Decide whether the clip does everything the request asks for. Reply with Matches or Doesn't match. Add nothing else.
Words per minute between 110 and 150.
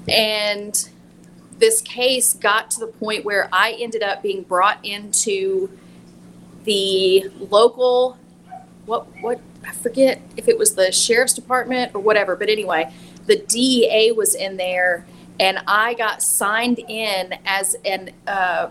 Matches